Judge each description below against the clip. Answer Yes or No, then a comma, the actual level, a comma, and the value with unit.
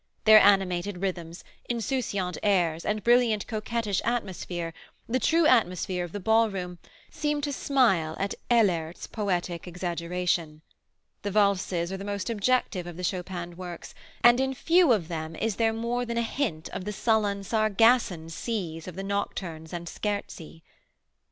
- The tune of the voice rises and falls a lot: No, average, 4.5 semitones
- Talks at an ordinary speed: Yes, average, 150 wpm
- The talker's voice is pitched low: No, high, 195 Hz